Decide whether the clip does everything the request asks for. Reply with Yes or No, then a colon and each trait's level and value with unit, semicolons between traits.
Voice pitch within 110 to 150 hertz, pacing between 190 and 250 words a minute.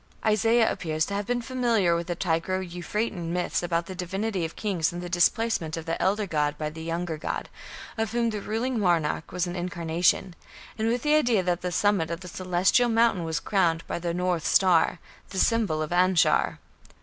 No: medium, 180 Hz; average, 195 wpm